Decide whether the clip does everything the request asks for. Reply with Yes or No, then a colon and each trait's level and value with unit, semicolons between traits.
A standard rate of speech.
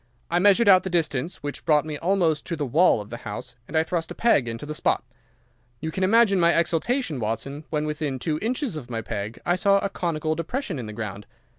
No: fast, 230 wpm